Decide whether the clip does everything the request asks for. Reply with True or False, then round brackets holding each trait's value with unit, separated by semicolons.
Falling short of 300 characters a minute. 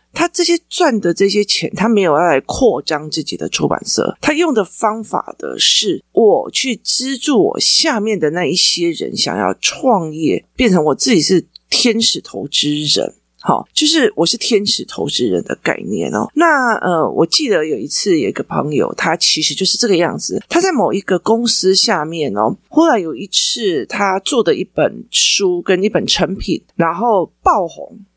True (260 characters per minute)